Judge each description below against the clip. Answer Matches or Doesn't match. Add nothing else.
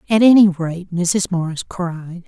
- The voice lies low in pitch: Doesn't match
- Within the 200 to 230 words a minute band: Doesn't match